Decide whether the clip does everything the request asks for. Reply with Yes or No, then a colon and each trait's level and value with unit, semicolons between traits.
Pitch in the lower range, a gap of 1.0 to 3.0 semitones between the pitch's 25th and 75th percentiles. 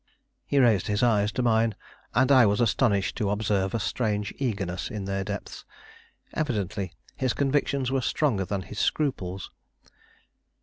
No: low, 105 Hz; average, 4.2 semitones